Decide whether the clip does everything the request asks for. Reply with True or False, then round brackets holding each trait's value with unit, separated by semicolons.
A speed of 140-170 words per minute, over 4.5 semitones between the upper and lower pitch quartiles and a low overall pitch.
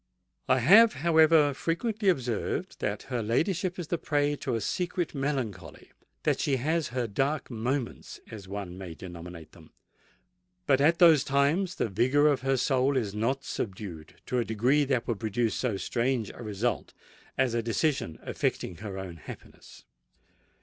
True (155 wpm; 5.4 semitones; 130 Hz)